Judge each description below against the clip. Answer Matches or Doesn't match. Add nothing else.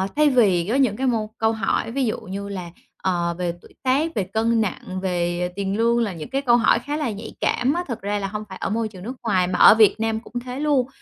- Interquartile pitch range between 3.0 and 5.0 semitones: Matches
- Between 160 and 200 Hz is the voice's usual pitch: Doesn't match